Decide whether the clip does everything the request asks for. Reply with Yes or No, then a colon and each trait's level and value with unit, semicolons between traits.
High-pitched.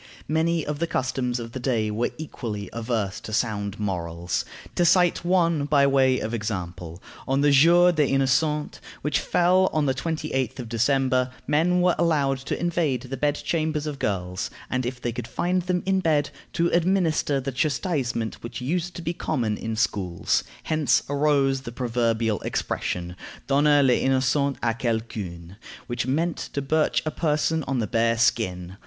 No: low, 135 Hz